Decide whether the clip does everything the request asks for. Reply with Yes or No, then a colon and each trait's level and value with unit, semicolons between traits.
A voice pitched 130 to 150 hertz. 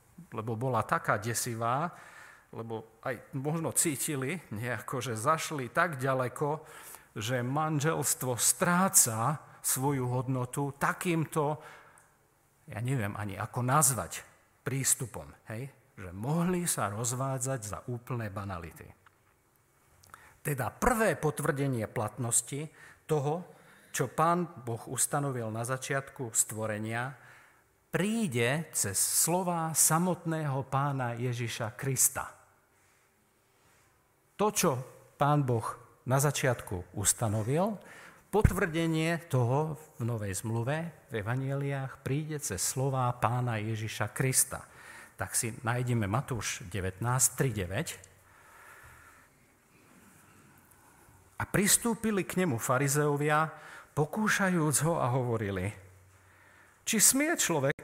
Yes: low, 135 Hz